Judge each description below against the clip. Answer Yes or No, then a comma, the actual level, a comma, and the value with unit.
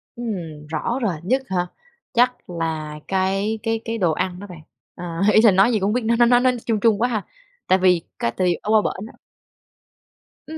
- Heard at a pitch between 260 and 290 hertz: No, high, 205 Hz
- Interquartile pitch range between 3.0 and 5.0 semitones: Yes, average, 4.5 semitones